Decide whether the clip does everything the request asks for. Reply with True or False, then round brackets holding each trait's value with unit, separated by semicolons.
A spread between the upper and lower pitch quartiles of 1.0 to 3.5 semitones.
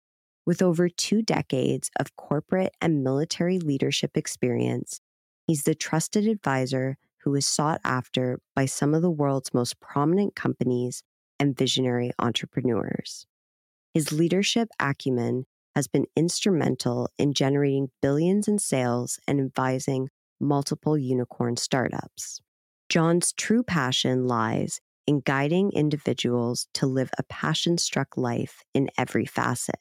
False (4.4 semitones)